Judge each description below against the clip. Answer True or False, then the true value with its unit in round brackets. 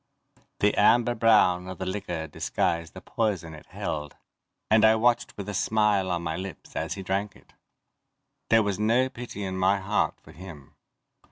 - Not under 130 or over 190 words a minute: True (175 wpm)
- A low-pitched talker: True (100 Hz)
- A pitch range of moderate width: True (3.3 semitones)